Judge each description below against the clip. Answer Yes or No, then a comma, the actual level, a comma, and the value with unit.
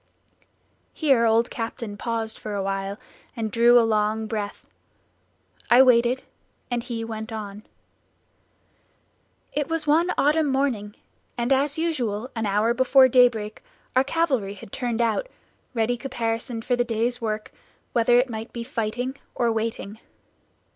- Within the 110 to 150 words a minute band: Yes, slow, 135 wpm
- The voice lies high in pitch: Yes, high, 235 Hz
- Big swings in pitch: No, average, 2.8 semitones